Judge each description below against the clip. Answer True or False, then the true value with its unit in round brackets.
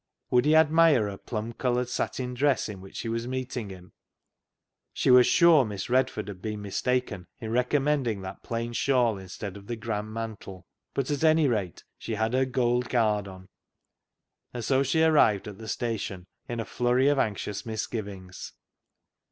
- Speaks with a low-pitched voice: True (115 Hz)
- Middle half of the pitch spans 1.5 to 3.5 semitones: False (3.9 semitones)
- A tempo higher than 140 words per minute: True (170 wpm)